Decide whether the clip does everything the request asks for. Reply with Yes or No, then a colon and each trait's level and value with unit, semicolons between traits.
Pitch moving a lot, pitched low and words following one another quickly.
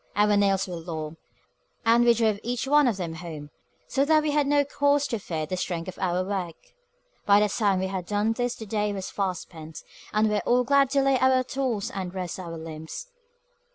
No: wide, 5.7 semitones; high, 205 Hz; fast, 225 wpm